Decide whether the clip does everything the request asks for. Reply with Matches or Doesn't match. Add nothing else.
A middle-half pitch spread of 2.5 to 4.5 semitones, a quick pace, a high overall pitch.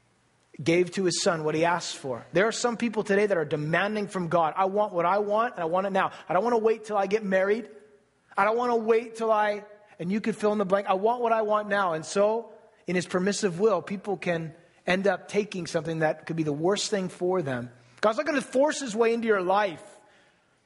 Matches